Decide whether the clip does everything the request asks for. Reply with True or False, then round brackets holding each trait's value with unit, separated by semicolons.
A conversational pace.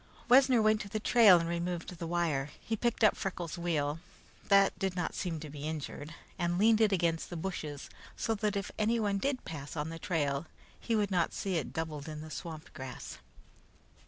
True (195 wpm)